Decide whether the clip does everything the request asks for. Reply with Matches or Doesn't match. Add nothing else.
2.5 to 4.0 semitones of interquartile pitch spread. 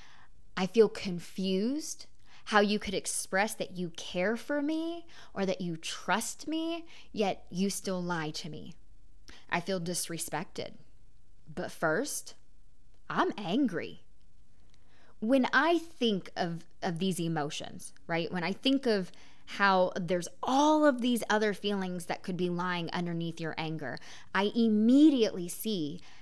Doesn't match